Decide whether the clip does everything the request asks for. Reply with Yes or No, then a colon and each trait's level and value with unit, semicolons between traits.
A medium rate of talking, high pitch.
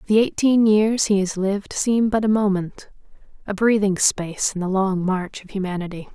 Yes: average, 185 wpm; high, 200 Hz